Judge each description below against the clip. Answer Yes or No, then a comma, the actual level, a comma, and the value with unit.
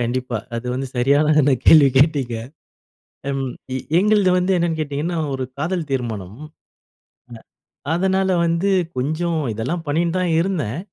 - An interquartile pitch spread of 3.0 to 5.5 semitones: Yes, average, 4.9 semitones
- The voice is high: No, medium, 155 Hz